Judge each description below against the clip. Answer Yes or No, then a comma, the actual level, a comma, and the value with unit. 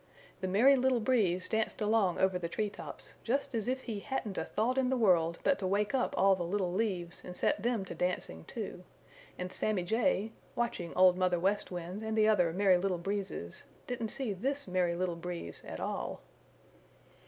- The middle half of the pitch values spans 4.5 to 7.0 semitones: No, average, 3.8 semitones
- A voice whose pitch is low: No, high, 195 Hz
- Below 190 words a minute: No, average, 195 wpm